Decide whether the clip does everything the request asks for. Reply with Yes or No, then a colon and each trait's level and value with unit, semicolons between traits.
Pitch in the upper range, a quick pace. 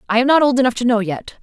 Yes: high, 240 Hz; fast, 340 wpm